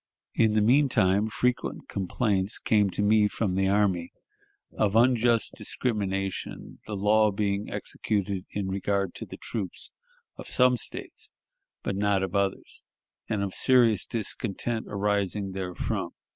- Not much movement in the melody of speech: Yes, narrow, 2.2 semitones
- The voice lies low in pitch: Yes, low, 105 Hz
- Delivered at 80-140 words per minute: Yes, slow, 135 wpm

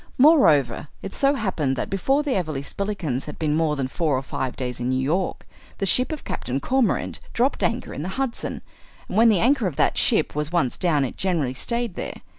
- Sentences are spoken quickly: Yes, fast, 215 wpm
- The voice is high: No, medium, 175 Hz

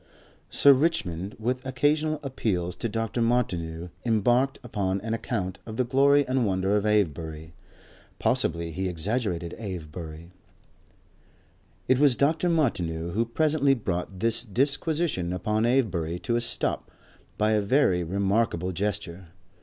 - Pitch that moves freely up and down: Yes, wide, 6.2 semitones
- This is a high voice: No, low, 105 Hz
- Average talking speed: No, slow, 130 wpm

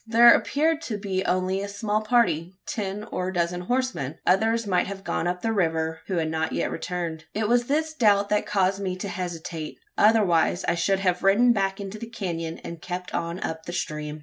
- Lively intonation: No, average, 3.9 semitones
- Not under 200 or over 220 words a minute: Yes, fast, 205 wpm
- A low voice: No, high, 190 Hz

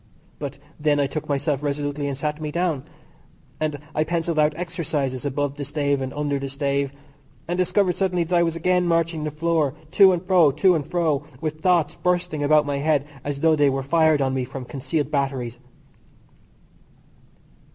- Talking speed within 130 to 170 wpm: No, average, 185 wpm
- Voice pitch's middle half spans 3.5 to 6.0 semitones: No, average, 3.0 semitones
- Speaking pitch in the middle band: Yes, medium, 150 Hz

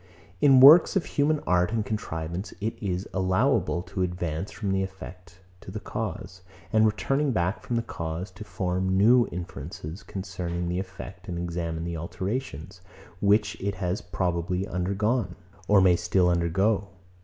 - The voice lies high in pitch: No, very low, 95 Hz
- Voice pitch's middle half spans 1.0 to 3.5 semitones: Yes, average, 3.1 semitones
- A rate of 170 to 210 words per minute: No, average, 155 wpm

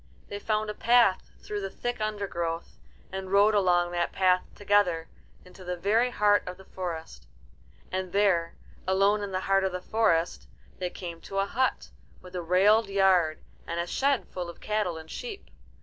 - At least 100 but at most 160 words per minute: No, average, 180 wpm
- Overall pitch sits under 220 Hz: Yes, high, 190 Hz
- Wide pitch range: No, average, 2.8 semitones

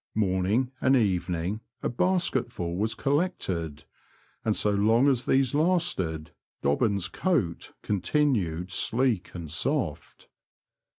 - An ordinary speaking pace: No, slow, 110 wpm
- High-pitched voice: No, low, 105 Hz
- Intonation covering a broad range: Yes, wide, 7.2 semitones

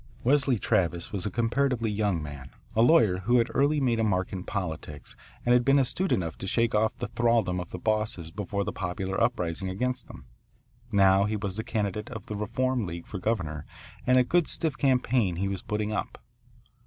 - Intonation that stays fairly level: No, average, 4.5 semitones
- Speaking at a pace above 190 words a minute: Yes, average, 200 wpm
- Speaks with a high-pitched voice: No, low, 105 Hz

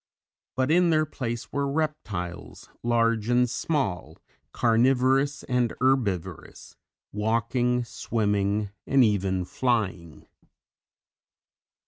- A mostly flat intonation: No, average, 4.3 semitones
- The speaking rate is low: Yes, slow, 85 wpm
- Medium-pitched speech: No, low, 120 Hz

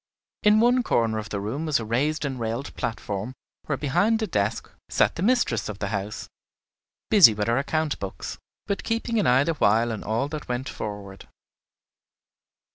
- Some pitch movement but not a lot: No, wide, 6.7 semitones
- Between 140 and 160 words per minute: No, average, 180 wpm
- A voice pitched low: Yes, low, 125 Hz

